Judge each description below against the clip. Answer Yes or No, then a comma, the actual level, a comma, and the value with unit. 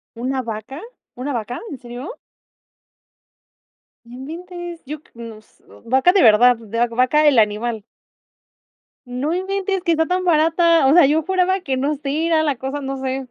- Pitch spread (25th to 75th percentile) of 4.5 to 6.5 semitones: Yes, average, 5.2 semitones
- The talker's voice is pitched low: No, very high, 275 Hz